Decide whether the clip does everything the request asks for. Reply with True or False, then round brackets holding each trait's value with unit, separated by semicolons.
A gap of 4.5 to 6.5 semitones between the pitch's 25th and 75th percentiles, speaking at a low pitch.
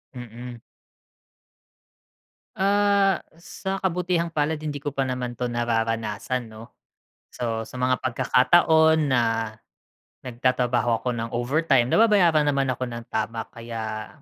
True (5.1 semitones; 125 Hz)